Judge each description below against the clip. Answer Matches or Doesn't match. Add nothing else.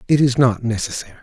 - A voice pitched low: Matches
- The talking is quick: Doesn't match